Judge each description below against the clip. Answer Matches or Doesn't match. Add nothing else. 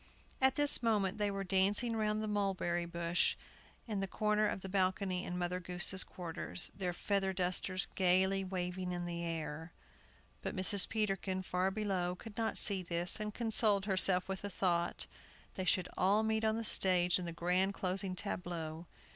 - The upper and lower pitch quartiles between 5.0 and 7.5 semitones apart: Doesn't match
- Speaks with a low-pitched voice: Doesn't match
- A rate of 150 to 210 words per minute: Matches